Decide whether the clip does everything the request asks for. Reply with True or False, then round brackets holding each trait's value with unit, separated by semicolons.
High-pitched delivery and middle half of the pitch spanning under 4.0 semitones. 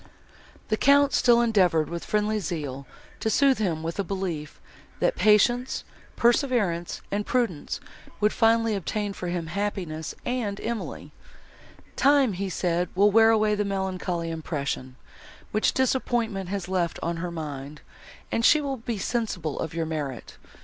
False (200 Hz; 5.3 semitones)